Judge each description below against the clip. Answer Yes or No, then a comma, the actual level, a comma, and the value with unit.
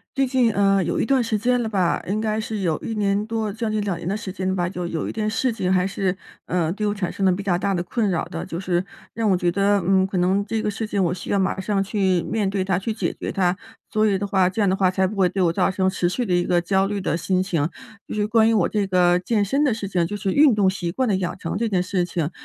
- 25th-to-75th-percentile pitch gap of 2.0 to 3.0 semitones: Yes, average, 2.7 semitones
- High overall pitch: Yes, high, 195 Hz